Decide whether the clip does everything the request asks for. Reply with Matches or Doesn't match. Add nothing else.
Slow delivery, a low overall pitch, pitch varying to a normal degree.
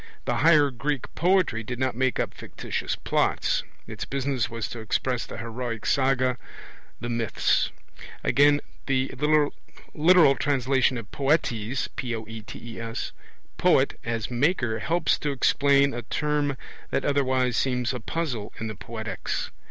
Matches